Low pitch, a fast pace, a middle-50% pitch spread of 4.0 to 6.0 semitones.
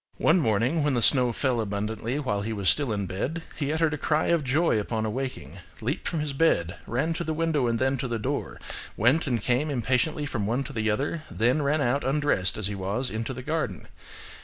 Yes: low, 130 Hz; fast, 220 wpm; average, 5.3 semitones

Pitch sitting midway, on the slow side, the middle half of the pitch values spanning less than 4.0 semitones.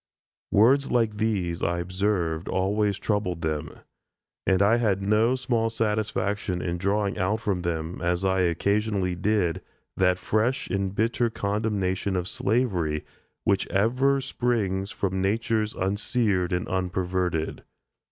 No: low, 100 Hz; slow, 125 wpm; average, 3.1 semitones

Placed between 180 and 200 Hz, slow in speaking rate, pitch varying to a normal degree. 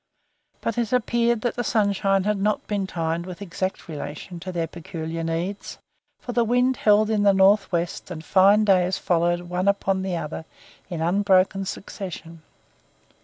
No: high, 190 Hz; average, 165 wpm; average, 3.3 semitones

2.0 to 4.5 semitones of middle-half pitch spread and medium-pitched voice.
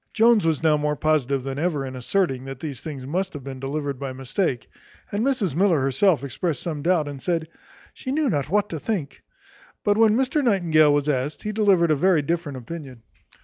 No: wide, 5.6 semitones; medium, 155 Hz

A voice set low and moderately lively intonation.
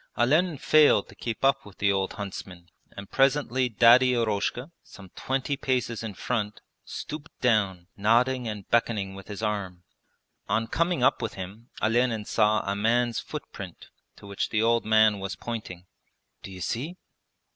Yes: low, 115 Hz; average, 3.9 semitones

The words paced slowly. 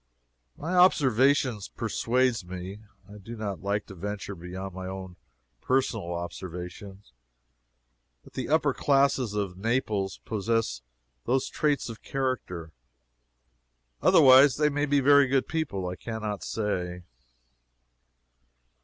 Yes: slow, 120 wpm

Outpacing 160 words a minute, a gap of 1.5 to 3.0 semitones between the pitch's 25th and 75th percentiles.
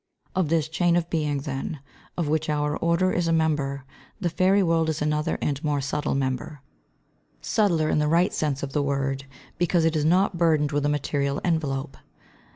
Yes: average, 190 wpm; average, 2.7 semitones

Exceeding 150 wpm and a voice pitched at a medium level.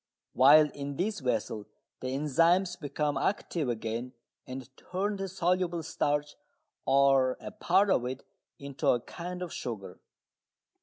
No: slow, 135 wpm; medium, 145 Hz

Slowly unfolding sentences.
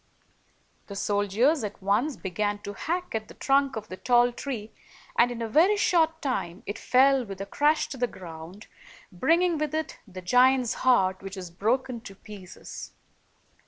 No: average, 170 wpm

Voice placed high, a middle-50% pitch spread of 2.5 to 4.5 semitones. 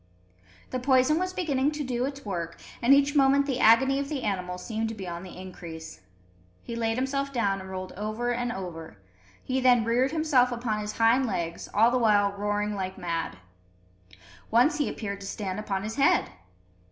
No: high, 230 Hz; average, 5.2 semitones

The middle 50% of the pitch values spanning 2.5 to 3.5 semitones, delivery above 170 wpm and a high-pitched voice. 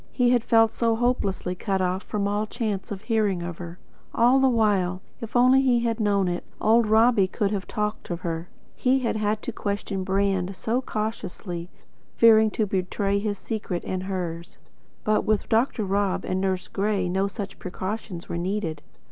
Yes: average, 3.1 semitones; average, 180 wpm; high, 205 Hz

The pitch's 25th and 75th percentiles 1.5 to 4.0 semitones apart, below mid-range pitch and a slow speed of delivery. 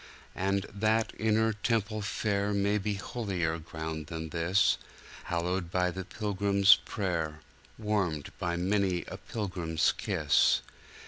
Yes: average, 3.5 semitones; very low, 95 Hz; slow, 115 wpm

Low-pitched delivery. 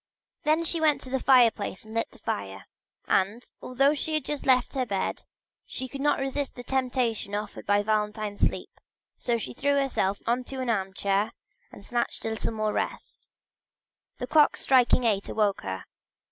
No: high, 240 Hz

